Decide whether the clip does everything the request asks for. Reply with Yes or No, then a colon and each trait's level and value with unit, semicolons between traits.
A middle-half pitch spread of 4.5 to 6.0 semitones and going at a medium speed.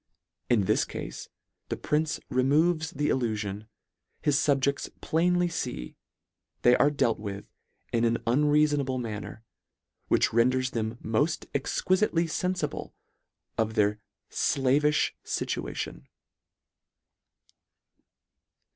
No: average, 5.0 semitones; slow, 95 wpm